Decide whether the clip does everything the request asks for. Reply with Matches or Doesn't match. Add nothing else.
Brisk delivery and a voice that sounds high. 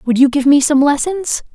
Matches